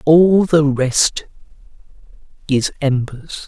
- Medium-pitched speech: Yes, medium, 145 Hz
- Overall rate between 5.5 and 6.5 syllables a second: No, 2.9 syllables/s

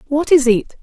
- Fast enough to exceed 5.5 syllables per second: No, 4.8 syllables/s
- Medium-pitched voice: No, very high, 275 Hz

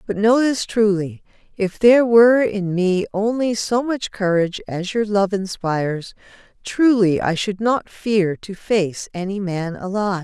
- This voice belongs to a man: No, female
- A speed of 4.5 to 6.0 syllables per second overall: No, 4.3 syllables/s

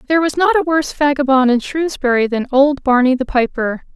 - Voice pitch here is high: Yes, very high, 275 Hz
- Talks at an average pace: Yes, average, 195 wpm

